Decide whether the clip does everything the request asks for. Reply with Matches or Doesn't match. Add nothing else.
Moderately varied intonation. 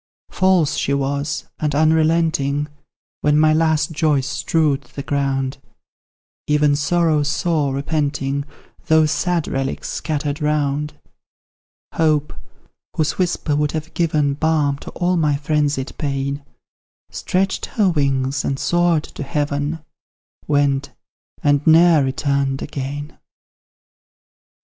Doesn't match